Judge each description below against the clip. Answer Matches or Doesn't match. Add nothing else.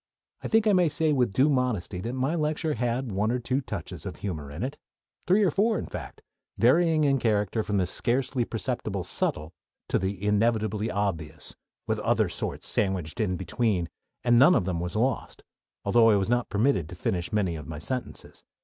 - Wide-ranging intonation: Matches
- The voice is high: Doesn't match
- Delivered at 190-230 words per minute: Matches